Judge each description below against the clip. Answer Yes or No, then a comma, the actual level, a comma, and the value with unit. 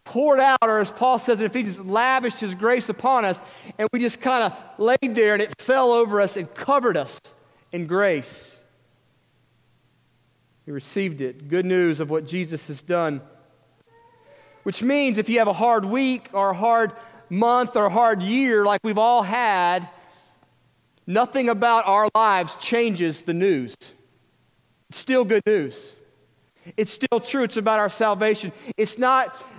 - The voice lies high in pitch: Yes, high, 215 Hz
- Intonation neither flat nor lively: No, wide, 5.7 semitones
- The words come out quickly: No, average, 160 wpm